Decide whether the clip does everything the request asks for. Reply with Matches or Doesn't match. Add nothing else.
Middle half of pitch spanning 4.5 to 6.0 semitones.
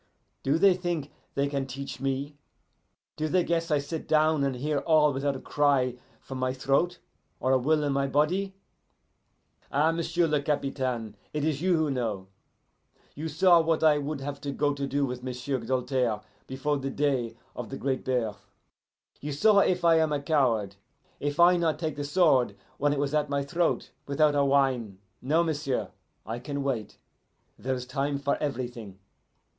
Doesn't match